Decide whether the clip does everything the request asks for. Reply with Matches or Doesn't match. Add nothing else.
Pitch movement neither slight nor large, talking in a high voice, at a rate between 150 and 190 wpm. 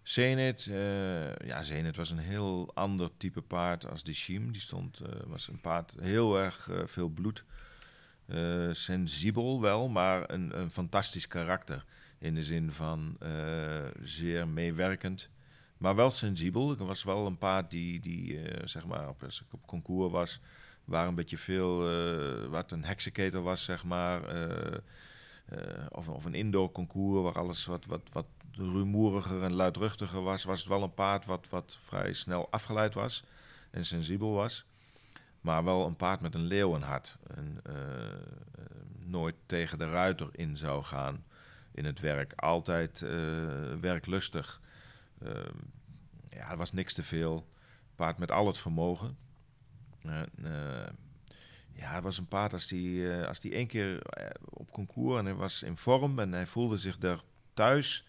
Doesn't match